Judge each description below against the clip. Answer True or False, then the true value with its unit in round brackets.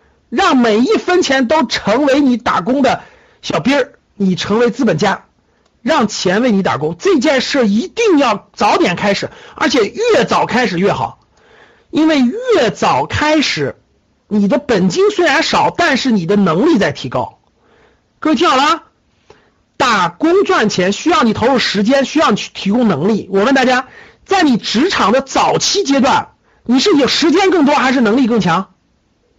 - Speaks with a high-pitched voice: True (265 Hz)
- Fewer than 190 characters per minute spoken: False (240 characters per minute)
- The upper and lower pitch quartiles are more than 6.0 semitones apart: True (6.5 semitones)